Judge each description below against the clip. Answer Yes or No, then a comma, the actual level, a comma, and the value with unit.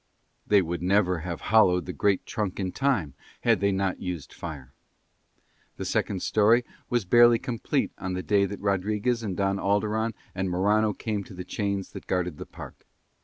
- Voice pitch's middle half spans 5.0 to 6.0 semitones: No, average, 2.8 semitones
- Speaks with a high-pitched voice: No, low, 100 Hz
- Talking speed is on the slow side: No, average, 175 wpm